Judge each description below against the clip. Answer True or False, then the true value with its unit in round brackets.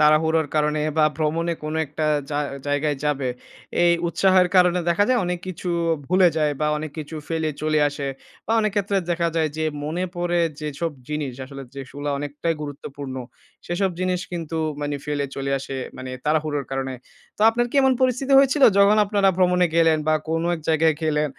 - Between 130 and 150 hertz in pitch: False (160 Hz)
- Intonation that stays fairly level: False (3.4 semitones)